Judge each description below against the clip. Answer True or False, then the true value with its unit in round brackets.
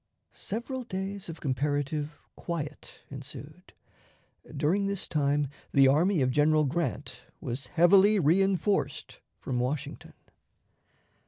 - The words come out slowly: True (100 wpm)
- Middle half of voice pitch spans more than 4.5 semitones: True (5.1 semitones)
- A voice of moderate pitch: True (155 Hz)